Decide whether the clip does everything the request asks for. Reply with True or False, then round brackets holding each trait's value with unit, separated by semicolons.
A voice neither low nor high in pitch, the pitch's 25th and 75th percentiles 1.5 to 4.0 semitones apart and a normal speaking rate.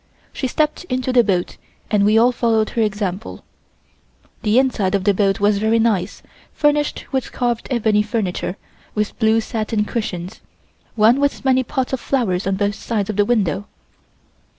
False (220 Hz; 3.2 semitones; 165 wpm)